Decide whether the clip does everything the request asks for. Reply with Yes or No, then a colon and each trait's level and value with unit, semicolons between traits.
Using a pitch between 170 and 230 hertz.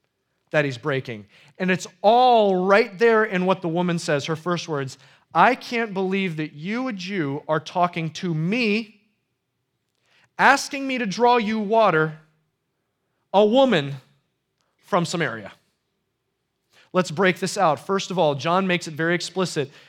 Yes: medium, 185 Hz